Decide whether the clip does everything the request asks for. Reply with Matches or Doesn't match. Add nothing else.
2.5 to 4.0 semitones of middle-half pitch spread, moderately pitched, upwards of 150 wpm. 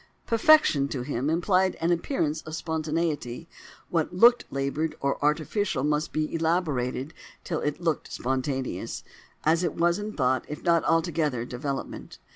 Doesn't match